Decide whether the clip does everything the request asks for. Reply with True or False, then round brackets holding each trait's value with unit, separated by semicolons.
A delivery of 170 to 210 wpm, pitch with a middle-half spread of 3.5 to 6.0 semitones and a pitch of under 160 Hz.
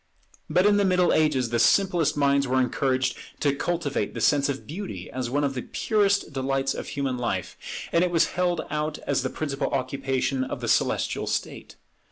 True (190 wpm; 4.6 semitones; 140 Hz)